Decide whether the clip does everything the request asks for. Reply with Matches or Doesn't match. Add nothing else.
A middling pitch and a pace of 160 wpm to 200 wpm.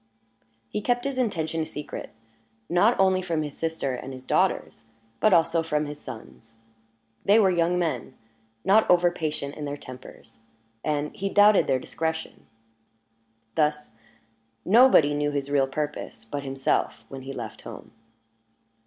Doesn't match